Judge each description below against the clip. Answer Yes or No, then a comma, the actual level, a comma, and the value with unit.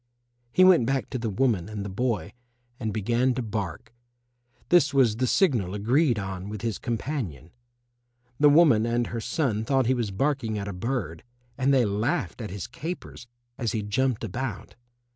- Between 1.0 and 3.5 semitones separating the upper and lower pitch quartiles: No, average, 4.4 semitones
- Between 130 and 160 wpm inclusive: No, average, 175 wpm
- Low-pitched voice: Yes, low, 115 Hz